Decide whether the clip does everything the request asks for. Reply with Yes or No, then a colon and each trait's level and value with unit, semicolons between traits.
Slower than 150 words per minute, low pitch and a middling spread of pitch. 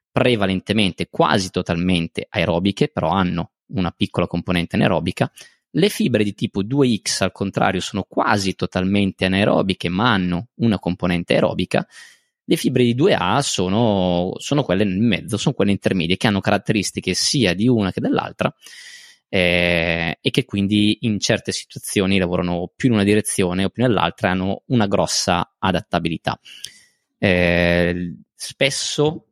Yes: average, 140 wpm; very low, 95 Hz; average, 3.9 semitones